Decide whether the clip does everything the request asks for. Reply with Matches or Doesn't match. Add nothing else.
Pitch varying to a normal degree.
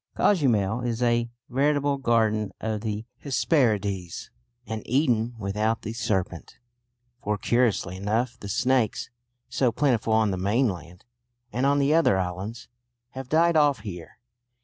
Matches